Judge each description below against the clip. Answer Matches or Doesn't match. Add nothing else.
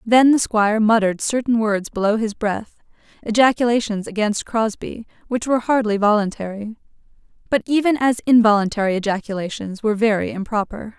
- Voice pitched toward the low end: Doesn't match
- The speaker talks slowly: Matches